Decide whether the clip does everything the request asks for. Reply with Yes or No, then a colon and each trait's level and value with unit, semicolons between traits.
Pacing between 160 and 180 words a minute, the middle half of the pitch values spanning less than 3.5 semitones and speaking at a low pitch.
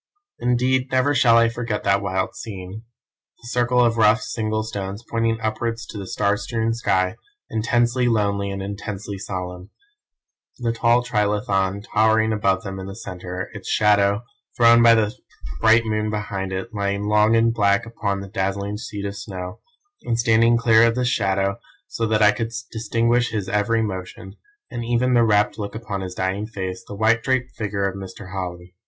Yes: average, 175 wpm; average, 2.8 semitones; low, 105 Hz